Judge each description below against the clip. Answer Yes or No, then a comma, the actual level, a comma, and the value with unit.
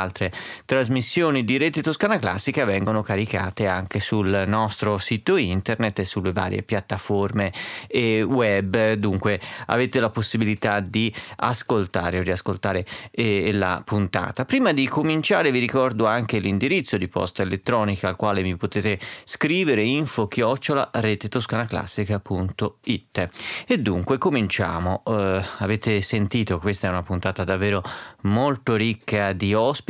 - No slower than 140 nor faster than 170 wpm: No, average, 125 wpm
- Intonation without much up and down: No, average, 3.1 semitones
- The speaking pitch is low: Yes, low, 105 Hz